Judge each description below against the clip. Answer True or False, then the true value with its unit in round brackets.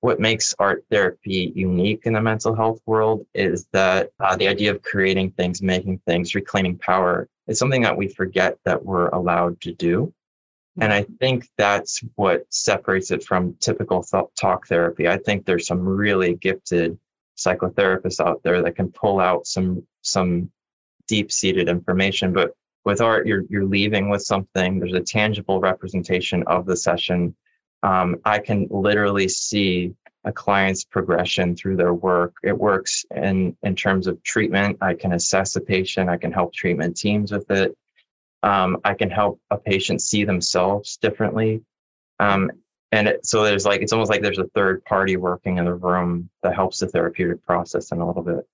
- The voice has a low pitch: True (95 Hz)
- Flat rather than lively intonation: True (2.3 semitones)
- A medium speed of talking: True (175 wpm)